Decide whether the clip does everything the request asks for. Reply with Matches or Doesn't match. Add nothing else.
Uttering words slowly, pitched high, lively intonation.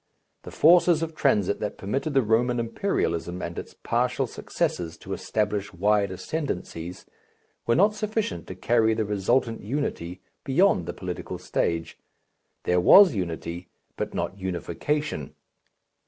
Doesn't match